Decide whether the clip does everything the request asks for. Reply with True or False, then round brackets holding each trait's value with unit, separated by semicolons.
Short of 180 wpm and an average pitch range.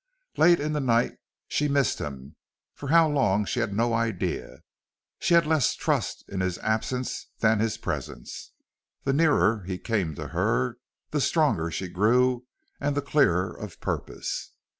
False (160 wpm; 6.6 semitones)